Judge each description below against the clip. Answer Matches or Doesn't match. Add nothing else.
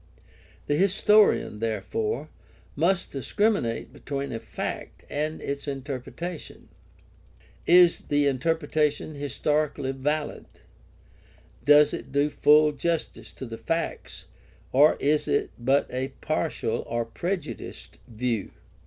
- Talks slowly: Matches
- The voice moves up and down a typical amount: Matches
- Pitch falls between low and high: Matches